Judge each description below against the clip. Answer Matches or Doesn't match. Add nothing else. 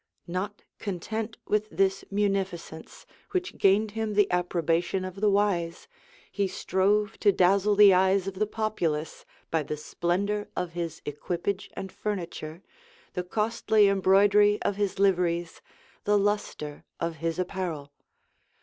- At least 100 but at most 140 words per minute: Matches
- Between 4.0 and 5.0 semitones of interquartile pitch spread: Doesn't match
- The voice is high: Matches